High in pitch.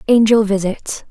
Yes: high, 210 Hz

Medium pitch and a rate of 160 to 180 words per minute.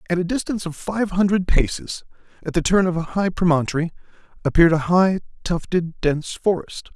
Yes: medium, 175 Hz; average, 175 wpm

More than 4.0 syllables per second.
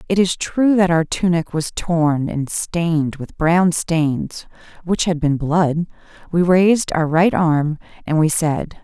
No: 3.7 syllables/s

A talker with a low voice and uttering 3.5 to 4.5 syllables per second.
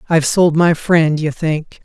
No: medium, 160 Hz; 4.3 syllables/s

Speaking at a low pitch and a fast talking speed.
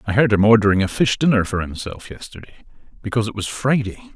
No: low, 110 Hz; average, 190 wpm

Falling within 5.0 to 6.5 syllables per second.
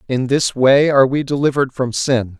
Yes: 5.4 syllables/s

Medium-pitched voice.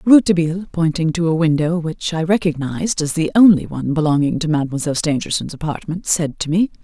Yes: medium, 165 Hz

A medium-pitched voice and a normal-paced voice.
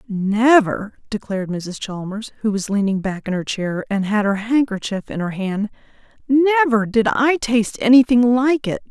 No: high, 220 Hz; average, 170 wpm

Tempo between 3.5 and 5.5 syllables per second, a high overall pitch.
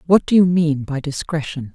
No: 5.0 syllables/s; medium, 160 Hz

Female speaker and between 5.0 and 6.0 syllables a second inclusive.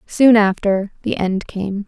No: female; 3.7 syllables/s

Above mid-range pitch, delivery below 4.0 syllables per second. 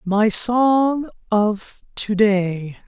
Yes: high, 215 Hz; 2.1 syllables/s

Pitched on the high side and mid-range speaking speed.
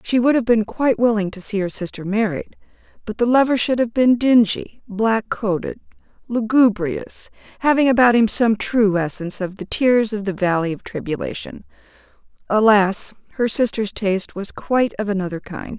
Yes: high, 215 Hz; average, 165 wpm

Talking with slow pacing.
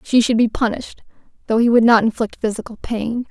No: average, 200 wpm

